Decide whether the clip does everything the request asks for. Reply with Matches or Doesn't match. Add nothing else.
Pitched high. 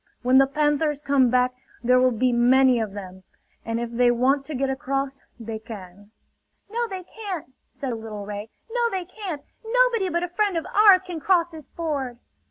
Matches